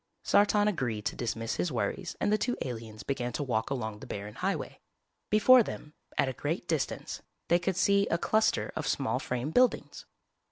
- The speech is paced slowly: No, average, 185 wpm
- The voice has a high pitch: No, medium, 145 Hz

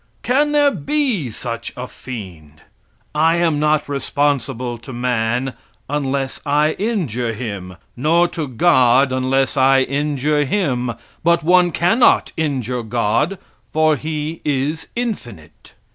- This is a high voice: No, medium, 140 Hz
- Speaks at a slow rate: Yes, slow, 120 wpm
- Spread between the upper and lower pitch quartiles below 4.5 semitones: No, average, 4.8 semitones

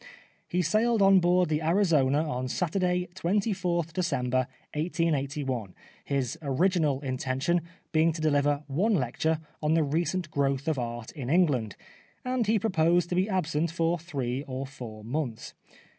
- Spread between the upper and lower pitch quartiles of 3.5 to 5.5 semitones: Yes, average, 4.7 semitones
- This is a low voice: No, medium, 155 Hz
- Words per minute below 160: Yes, average, 145 wpm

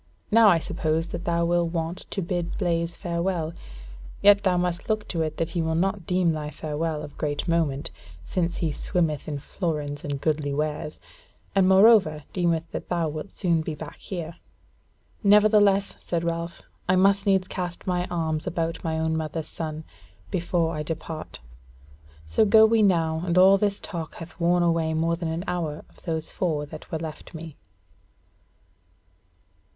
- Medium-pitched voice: Yes, medium, 170 Hz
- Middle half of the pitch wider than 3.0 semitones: No, narrow, 2.4 semitones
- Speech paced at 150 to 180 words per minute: Yes, average, 170 wpm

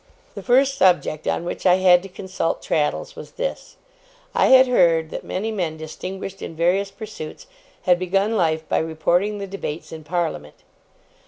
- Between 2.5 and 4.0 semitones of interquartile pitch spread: Yes, average, 3.6 semitones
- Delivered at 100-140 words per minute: No, average, 165 wpm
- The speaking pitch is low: No, medium, 180 Hz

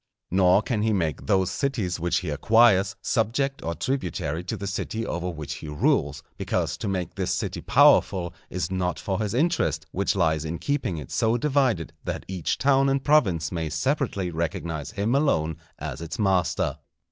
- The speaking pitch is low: Yes, very low, 95 Hz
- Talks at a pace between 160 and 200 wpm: Yes, average, 175 wpm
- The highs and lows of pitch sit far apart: Yes, wide, 5.7 semitones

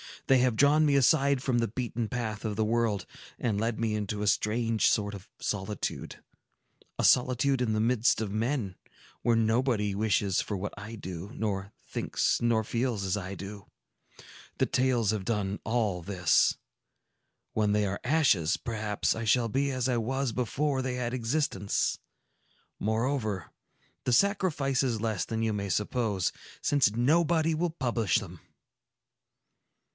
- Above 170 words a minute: No, average, 150 wpm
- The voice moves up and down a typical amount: Yes, average, 3.6 semitones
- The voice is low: Yes, low, 115 Hz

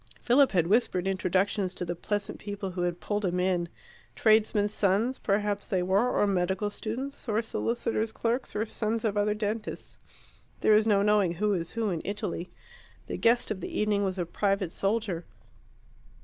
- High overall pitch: Yes, high, 205 Hz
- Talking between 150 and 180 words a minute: Yes, average, 175 wpm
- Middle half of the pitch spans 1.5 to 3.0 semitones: Yes, average, 2.7 semitones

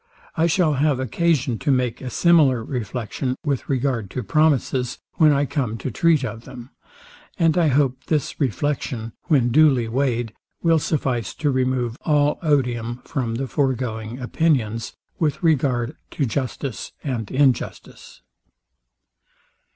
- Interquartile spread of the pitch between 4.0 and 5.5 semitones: No, average, 3.6 semitones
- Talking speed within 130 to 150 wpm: Yes, slow, 135 wpm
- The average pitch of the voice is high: No, low, 130 Hz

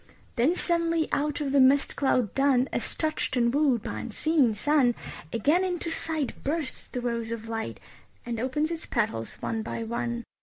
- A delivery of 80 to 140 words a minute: No, average, 175 wpm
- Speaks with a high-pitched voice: Yes, very high, 265 Hz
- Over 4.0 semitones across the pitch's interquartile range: Yes, average, 4.7 semitones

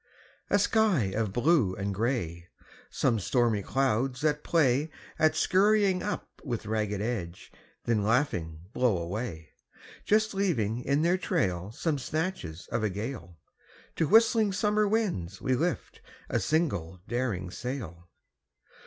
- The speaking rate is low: Yes, slow, 130 wpm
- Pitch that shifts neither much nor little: No, wide, 9.0 semitones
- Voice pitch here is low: Yes, low, 125 Hz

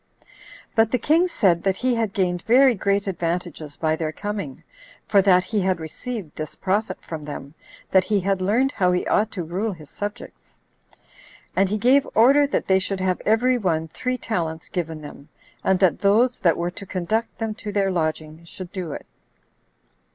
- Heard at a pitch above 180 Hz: Yes, high, 190 Hz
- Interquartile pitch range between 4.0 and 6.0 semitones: Yes, average, 4.5 semitones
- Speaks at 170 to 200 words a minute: Yes, average, 185 wpm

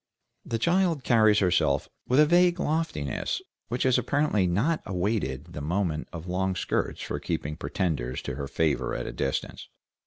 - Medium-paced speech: Yes, average, 160 wpm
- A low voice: Yes, very low, 95 Hz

